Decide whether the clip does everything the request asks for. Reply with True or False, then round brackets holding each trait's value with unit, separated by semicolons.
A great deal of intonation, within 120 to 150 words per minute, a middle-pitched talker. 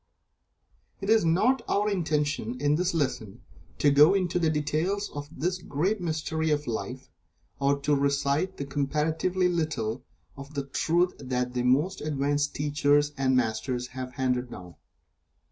False (3.7 semitones; 145 wpm; 145 Hz)